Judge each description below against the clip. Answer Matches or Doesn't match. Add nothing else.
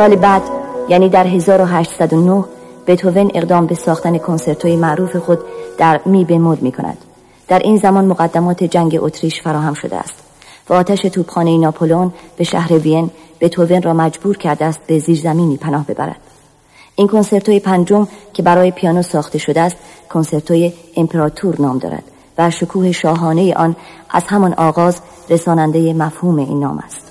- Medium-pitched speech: Matches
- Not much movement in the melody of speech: Matches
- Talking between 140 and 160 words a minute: Matches